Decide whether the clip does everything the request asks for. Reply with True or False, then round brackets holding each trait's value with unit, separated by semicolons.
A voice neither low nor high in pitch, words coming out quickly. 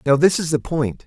True (150 Hz; 280 wpm)